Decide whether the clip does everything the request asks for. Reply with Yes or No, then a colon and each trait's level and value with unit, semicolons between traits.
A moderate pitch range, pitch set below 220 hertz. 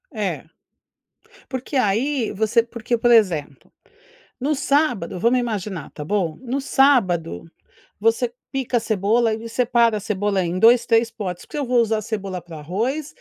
No: average, 4.2 semitones; high, 225 Hz